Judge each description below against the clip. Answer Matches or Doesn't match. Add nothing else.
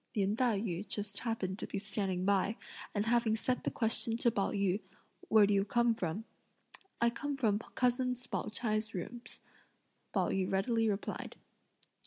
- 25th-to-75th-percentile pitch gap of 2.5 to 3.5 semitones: Matches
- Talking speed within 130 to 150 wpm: Doesn't match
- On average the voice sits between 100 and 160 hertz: Doesn't match